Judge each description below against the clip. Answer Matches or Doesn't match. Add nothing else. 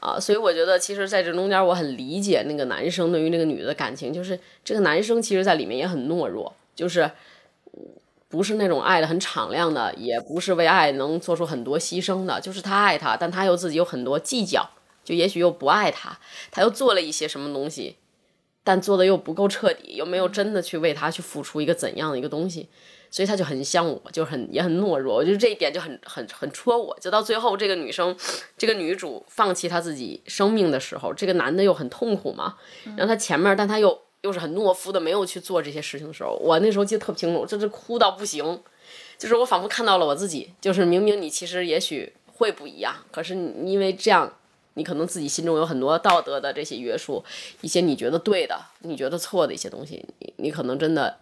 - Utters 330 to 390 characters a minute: Matches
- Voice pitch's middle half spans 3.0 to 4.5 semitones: Matches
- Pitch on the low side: Doesn't match